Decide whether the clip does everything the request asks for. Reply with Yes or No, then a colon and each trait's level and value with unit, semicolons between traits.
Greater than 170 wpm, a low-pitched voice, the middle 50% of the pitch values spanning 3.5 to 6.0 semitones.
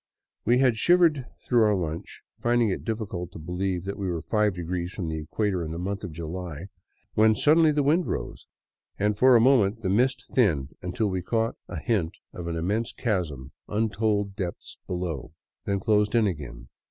Yes: average, 185 wpm; low, 100 Hz; average, 4.6 semitones